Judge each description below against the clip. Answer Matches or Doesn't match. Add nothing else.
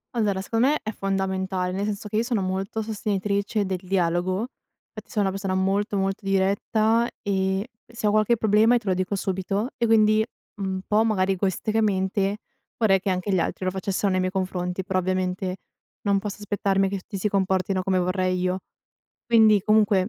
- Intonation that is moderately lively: Doesn't match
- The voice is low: Doesn't match